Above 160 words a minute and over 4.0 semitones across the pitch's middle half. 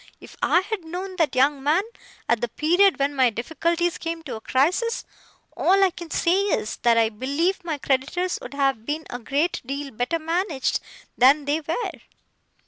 Yes: average, 180 wpm; average, 4.7 semitones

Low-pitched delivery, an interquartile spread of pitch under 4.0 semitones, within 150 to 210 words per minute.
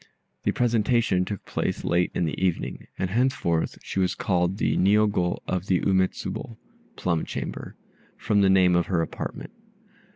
Yes: very low, 95 Hz; average, 2.8 semitones; average, 160 wpm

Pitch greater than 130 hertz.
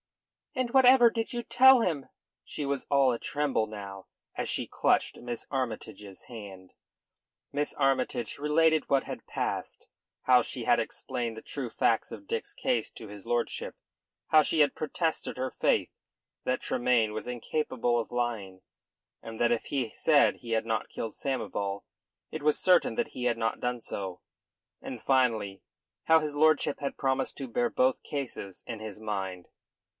No: low, 125 Hz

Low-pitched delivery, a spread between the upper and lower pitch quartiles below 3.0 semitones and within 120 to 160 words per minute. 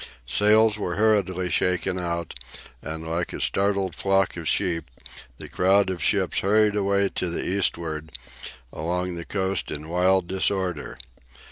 Yes: very low, 95 Hz; narrow, 2.6 semitones; average, 140 wpm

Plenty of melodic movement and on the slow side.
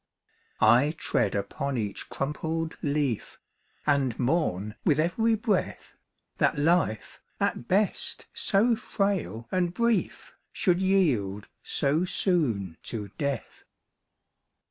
Yes: wide, 8.0 semitones; slow, 100 wpm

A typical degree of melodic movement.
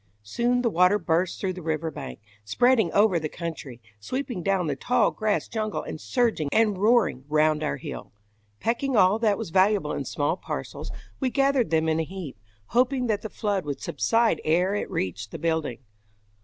No: wide, 6.2 semitones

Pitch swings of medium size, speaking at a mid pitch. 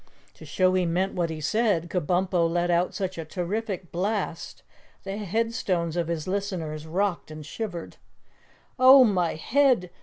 Yes: average, 3.1 semitones; medium, 180 Hz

